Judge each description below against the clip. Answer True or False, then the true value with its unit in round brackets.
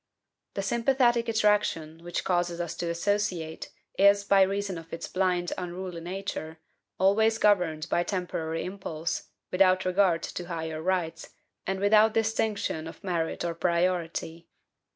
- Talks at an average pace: False (130 wpm)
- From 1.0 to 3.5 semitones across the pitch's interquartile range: True (3.2 semitones)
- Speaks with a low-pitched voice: False (180 Hz)